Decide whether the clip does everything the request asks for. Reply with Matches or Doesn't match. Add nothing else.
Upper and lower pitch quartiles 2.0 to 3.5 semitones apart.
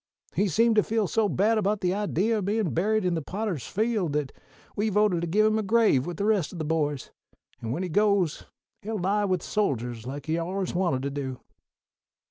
Doesn't match